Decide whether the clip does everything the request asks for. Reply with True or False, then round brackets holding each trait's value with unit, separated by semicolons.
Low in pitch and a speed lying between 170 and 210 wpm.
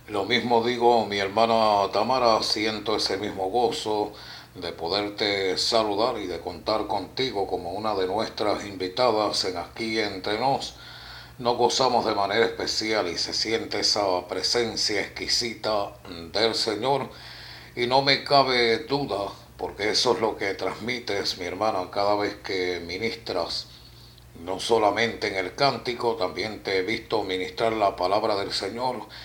False (110 Hz; 145 wpm)